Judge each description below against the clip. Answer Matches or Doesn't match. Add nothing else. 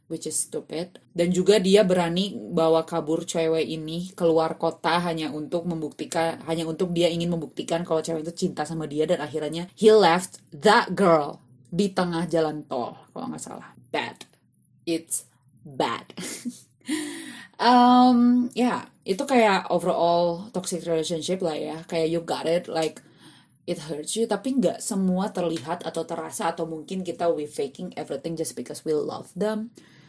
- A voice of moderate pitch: Matches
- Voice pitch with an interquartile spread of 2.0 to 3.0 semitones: Matches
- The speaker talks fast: Matches